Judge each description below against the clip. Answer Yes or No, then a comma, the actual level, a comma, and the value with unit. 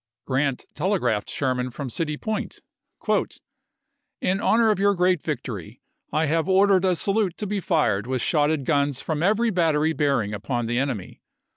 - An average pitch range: No, wide, 6.6 semitones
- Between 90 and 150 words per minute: No, average, 160 wpm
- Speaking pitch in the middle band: Yes, medium, 150 Hz